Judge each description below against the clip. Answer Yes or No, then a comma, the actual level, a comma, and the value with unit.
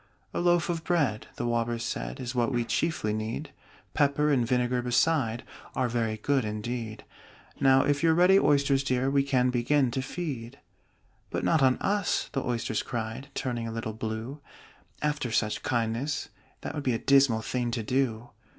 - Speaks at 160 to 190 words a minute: Yes, average, 170 wpm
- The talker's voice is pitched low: Yes, low, 125 Hz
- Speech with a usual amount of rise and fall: Yes, average, 3.6 semitones